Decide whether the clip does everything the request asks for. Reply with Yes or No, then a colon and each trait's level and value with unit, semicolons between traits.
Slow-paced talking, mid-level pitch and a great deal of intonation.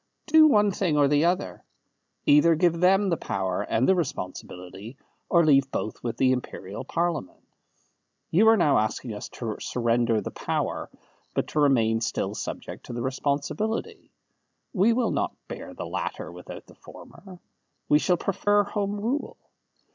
No: average, 155 wpm; medium, 150 Hz; wide, 8.7 semitones